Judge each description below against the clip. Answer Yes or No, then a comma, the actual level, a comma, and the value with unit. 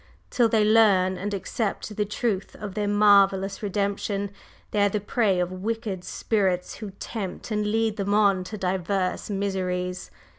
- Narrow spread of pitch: Yes, narrow, 2.0 semitones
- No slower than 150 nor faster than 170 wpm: Yes, average, 155 wpm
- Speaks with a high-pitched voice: Yes, high, 200 Hz